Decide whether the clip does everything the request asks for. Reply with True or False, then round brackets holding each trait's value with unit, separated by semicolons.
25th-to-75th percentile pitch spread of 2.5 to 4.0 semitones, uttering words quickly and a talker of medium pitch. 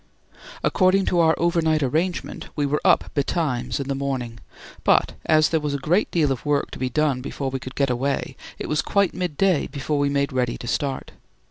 True (3.1 semitones; 210 wpm; 145 Hz)